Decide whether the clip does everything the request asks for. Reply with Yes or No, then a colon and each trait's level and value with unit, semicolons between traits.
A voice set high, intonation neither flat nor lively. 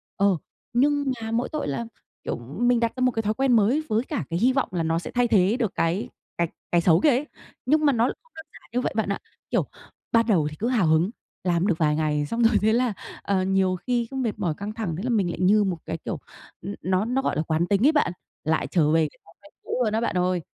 No: high, 210 Hz; wide, 5.8 semitones